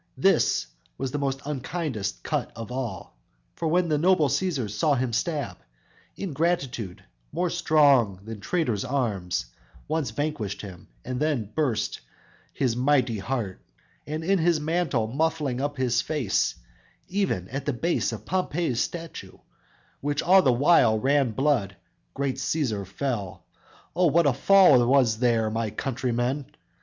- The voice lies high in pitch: No, low, 135 Hz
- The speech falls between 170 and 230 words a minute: No, average, 140 wpm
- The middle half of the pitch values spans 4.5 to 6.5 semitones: Yes, average, 5.3 semitones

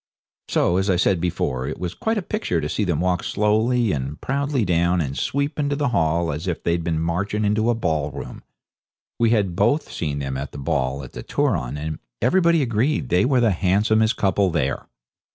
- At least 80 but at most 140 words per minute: No, average, 200 wpm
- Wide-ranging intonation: Yes, wide, 6.7 semitones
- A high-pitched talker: No, very low, 95 Hz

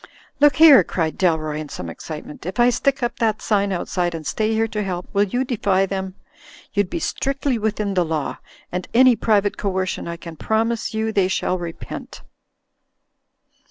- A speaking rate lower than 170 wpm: No, average, 175 wpm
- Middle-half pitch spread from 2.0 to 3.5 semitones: No, average, 4.2 semitones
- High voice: Yes, high, 200 Hz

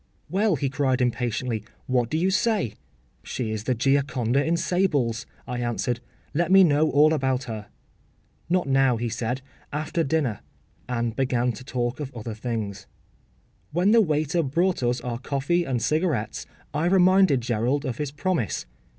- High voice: No, low, 135 Hz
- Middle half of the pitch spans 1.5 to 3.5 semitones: No, average, 5.0 semitones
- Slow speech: No, average, 160 wpm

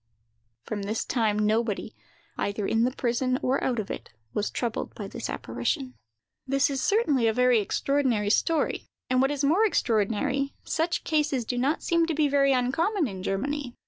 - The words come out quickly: No, average, 175 wpm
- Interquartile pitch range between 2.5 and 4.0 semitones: No, average, 4.7 semitones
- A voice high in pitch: Yes, very high, 255 Hz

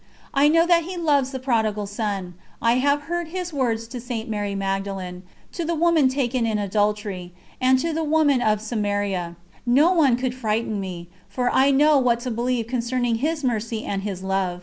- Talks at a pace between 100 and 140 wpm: No, average, 190 wpm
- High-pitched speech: Yes, high, 240 Hz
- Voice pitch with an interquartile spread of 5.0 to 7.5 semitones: Yes, wide, 5.4 semitones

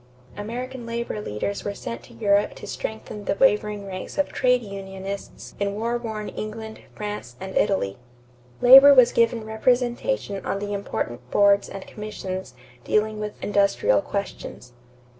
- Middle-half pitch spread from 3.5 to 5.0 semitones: No, average, 2.7 semitones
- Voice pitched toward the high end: Yes, high, 210 Hz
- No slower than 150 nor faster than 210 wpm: No, average, 140 wpm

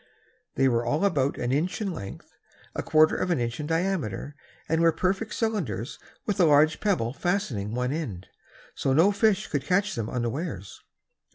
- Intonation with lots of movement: Yes, wide, 7.4 semitones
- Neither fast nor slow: Yes, average, 175 wpm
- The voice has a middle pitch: Yes, medium, 155 Hz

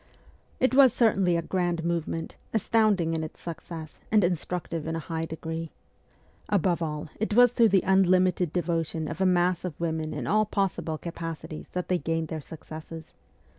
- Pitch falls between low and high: Yes, medium, 170 Hz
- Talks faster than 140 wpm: Yes, average, 170 wpm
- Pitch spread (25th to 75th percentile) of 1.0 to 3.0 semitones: Yes, narrow, 2.6 semitones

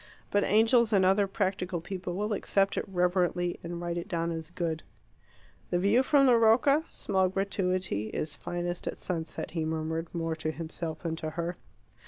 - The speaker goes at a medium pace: Yes, average, 175 wpm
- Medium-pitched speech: Yes, medium, 180 Hz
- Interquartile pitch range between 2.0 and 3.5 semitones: Yes, average, 3.1 semitones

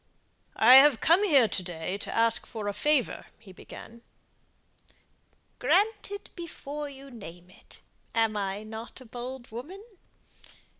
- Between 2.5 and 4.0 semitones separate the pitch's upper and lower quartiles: No, average, 5.3 semitones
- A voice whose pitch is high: Yes, high, 245 Hz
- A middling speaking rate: No, slow, 120 wpm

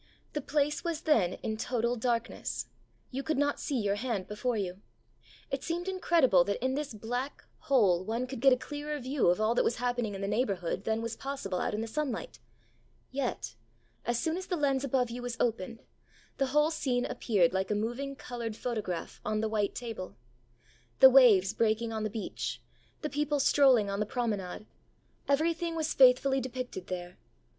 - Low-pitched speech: No, high, 245 Hz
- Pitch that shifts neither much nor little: Yes, average, 4.5 semitones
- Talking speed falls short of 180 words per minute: No, average, 185 wpm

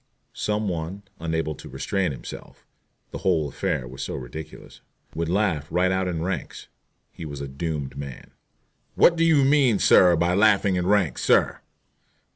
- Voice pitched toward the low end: Yes, very low, 85 Hz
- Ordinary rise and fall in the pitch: Yes, average, 4.5 semitones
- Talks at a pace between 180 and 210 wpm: No, average, 160 wpm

